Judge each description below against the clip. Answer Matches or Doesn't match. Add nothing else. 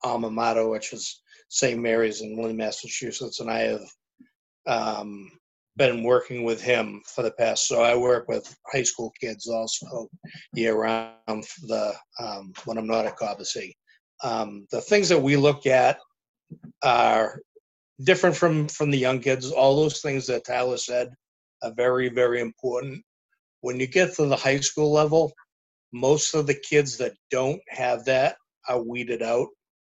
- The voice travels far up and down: Doesn't match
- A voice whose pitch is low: Matches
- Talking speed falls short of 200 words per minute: Matches